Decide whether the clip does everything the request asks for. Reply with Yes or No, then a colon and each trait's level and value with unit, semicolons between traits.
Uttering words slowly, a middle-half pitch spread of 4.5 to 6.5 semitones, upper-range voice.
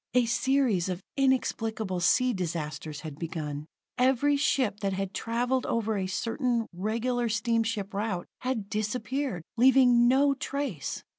Yes: slow, 130 wpm; average, 5.1 semitones; high, 225 Hz